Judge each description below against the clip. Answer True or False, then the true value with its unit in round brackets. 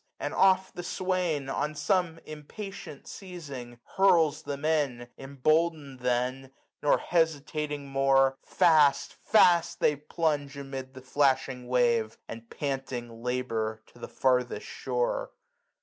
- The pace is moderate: False (120 wpm)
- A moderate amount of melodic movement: True (4.1 semitones)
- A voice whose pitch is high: False (140 Hz)